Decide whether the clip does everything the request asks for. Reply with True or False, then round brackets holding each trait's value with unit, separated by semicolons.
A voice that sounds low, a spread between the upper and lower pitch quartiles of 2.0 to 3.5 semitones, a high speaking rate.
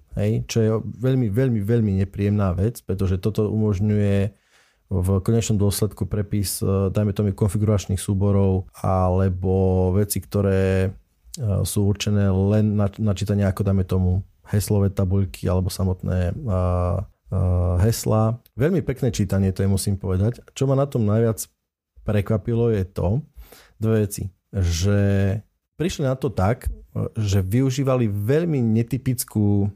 False (100 Hz; 2.6 semitones; 130 wpm)